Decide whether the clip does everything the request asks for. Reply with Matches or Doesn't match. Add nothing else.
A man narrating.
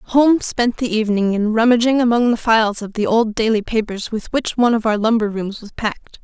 Doesn't match